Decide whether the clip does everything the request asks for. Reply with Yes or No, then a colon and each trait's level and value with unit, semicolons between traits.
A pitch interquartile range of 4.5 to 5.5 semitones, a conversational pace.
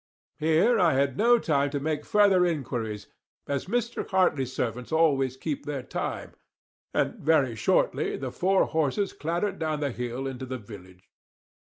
Yes: average, 5.0 semitones; average, 155 wpm